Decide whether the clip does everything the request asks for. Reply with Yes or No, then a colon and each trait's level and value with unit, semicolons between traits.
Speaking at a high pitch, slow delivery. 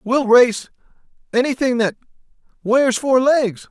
Yes: high, 245 Hz; slow, 80 wpm